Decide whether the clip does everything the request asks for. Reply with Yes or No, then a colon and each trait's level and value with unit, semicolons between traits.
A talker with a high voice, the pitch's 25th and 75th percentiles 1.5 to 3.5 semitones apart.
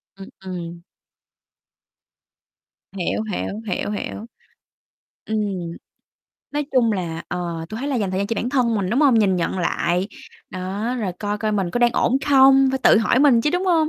No: high, 215 Hz; wide, 5.4 semitones